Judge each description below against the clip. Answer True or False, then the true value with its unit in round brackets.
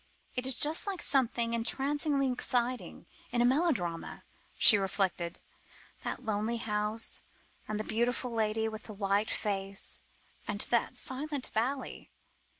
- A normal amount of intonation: True (3.6 semitones)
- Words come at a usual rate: False (130 wpm)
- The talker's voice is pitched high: True (230 Hz)